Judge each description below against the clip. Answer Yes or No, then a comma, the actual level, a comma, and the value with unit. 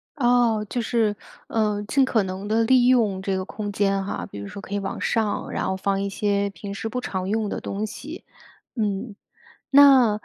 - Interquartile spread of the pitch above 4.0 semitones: No, average, 2.9 semitones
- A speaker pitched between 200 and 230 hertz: Yes, high, 210 Hz